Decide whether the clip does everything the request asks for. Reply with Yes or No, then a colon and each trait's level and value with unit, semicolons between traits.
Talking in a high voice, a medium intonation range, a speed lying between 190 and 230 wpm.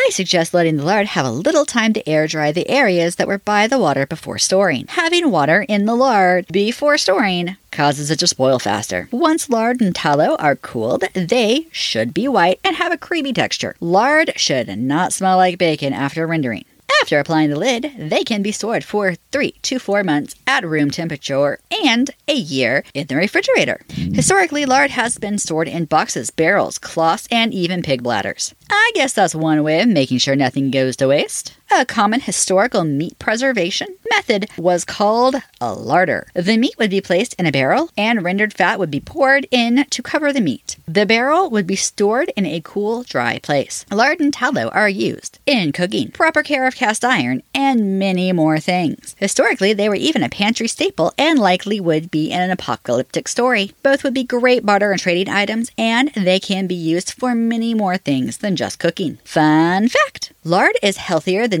No: high, 205 Hz; wide, 7.2 semitones; average, 195 wpm